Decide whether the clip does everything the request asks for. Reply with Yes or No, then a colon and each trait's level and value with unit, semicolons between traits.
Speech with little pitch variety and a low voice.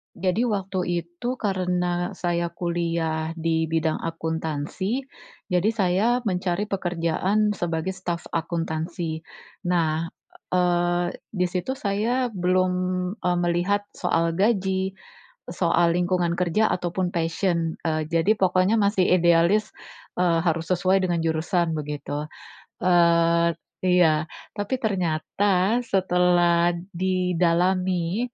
No: narrow, 2.1 semitones; medium, 175 Hz